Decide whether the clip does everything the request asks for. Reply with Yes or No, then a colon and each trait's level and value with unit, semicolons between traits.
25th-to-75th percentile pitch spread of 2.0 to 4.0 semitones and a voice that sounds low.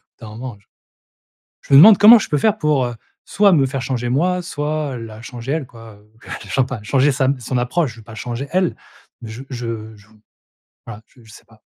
No: average, 4.6 semitones; low, 130 Hz